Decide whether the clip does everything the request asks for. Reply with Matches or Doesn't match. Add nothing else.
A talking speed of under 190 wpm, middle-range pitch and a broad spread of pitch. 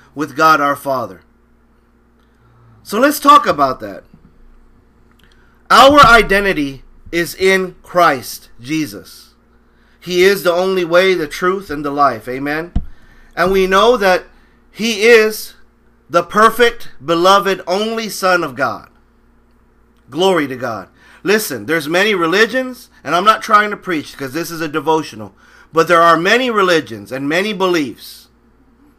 Matches